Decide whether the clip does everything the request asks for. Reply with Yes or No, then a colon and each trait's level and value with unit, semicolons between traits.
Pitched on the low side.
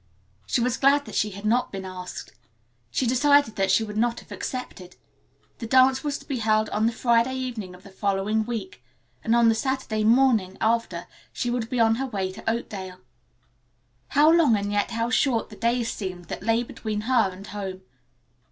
No: high, 225 Hz